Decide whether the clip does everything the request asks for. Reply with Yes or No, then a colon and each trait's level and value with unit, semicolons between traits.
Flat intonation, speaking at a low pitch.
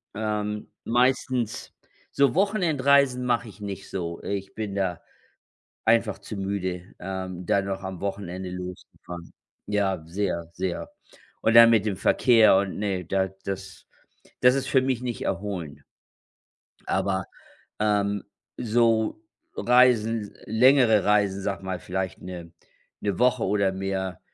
No: average, 3.4 semitones; low, 100 Hz